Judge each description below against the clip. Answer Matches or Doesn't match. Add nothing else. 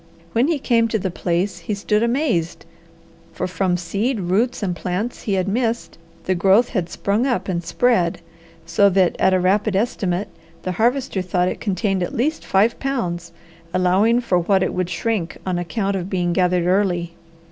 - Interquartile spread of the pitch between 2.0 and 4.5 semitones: Matches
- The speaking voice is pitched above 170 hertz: Matches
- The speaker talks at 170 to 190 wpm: Matches